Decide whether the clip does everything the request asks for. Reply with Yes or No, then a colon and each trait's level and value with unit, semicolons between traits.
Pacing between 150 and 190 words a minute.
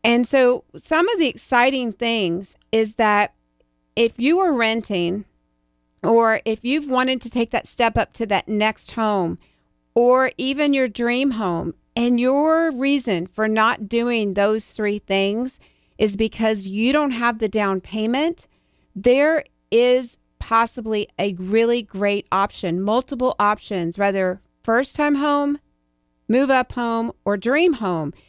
No: average, 140 wpm